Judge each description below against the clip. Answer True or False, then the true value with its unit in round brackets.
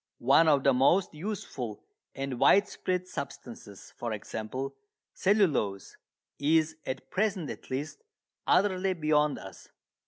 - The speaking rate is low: True (115 wpm)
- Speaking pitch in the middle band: True (150 Hz)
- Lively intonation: True (6.1 semitones)